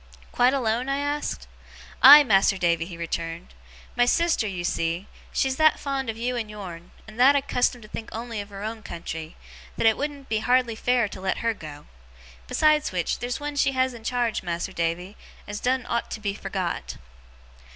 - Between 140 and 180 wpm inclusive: No, average, 190 wpm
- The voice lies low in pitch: No, high, 225 Hz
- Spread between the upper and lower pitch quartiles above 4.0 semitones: Yes, wide, 5.6 semitones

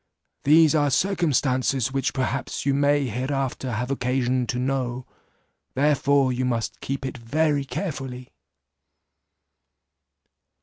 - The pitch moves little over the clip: Yes, narrow, 2.1 semitones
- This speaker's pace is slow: Yes, slow, 105 wpm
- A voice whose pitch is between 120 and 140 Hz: Yes, low, 135 Hz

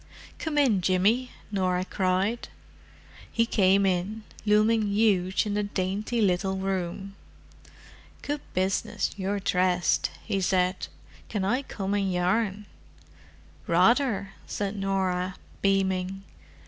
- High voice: Yes, high, 195 Hz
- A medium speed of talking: No, slow, 105 wpm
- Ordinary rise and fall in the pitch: No, narrow, 2.2 semitones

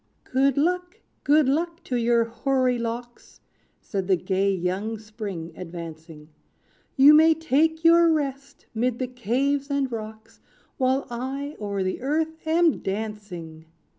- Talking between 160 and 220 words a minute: No, slow, 135 wpm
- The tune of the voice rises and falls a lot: Yes, wide, 5.9 semitones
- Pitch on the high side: Yes, very high, 250 Hz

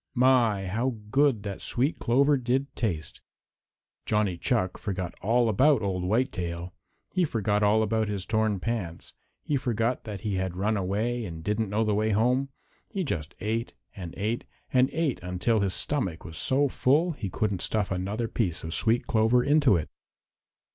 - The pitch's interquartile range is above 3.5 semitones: Yes, average, 4.4 semitones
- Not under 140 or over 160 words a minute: No, average, 170 wpm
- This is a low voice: Yes, low, 110 Hz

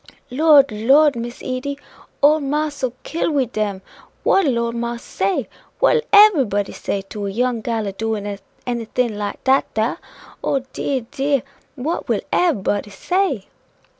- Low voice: No, high, 245 Hz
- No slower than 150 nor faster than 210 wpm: Yes, average, 160 wpm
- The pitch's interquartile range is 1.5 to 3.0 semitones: No, average, 4.9 semitones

